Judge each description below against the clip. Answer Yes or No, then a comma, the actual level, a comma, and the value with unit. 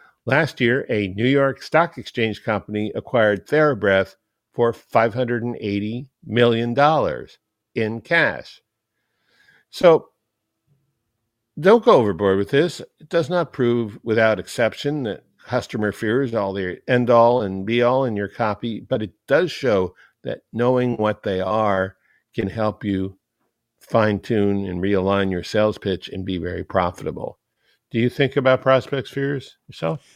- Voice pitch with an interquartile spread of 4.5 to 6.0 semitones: No, average, 3.9 semitones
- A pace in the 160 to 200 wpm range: No, average, 145 wpm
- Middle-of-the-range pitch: No, low, 115 Hz